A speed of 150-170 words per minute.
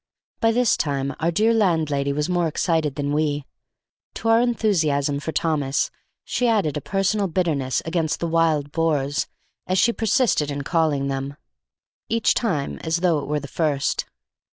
Yes: average, 160 wpm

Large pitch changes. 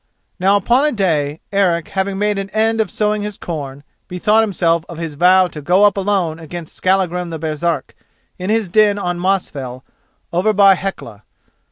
No: average, 3.5 semitones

